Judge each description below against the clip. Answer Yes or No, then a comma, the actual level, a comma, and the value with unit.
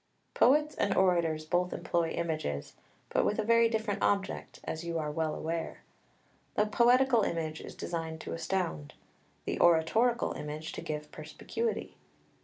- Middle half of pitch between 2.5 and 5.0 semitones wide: No, wide, 5.5 semitones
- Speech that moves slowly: No, average, 155 wpm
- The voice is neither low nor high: Yes, medium, 170 Hz